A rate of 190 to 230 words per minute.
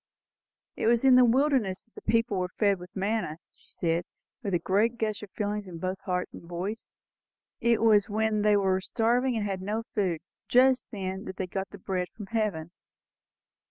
Yes: average, 195 wpm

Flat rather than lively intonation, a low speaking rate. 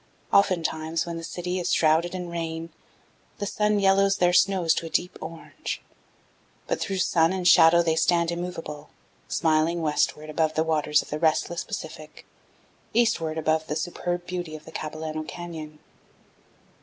No: narrow, 2.1 semitones; average, 155 wpm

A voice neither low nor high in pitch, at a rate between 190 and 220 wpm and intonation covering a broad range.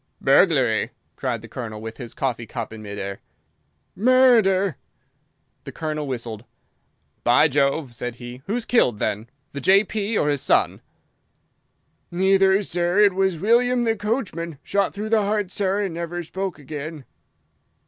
No: medium, 170 Hz; average, 145 wpm; wide, 8.1 semitones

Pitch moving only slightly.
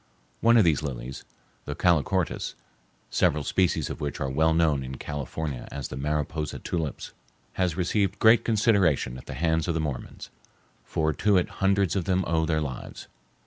No: average, 4.3 semitones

